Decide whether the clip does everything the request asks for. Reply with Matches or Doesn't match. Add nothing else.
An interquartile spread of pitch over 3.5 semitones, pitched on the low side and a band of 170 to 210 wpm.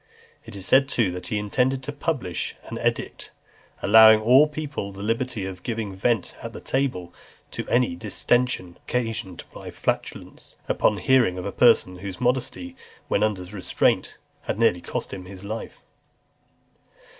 Doesn't match